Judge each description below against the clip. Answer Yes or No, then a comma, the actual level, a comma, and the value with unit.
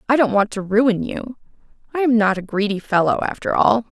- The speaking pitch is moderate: No, high, 220 Hz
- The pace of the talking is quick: Yes, fast, 210 wpm